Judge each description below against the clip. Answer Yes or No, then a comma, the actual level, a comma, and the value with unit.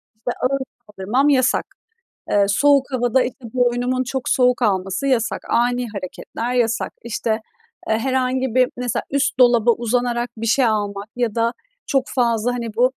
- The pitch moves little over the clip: Yes, narrow, 2.0 semitones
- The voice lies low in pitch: No, high, 245 Hz